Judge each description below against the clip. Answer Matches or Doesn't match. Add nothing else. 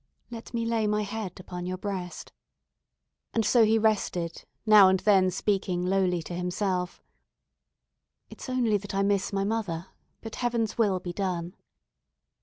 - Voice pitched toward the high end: Matches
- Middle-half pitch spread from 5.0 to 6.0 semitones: Doesn't match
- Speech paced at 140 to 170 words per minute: Matches